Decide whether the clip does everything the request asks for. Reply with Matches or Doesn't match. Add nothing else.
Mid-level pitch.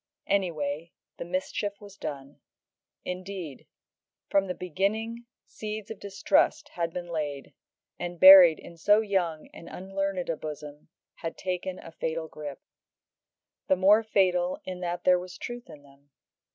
Matches